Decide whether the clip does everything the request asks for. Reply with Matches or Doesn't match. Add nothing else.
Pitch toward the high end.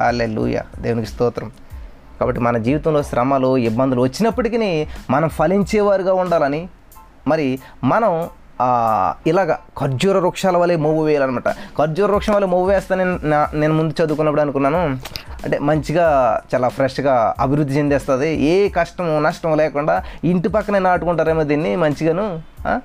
Doesn't match